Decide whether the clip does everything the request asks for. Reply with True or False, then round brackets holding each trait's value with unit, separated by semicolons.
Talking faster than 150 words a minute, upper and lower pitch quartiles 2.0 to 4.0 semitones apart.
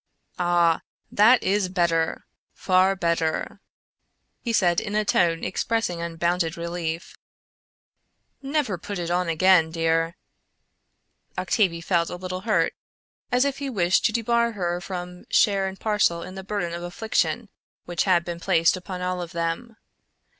False (145 wpm; 3.1 semitones)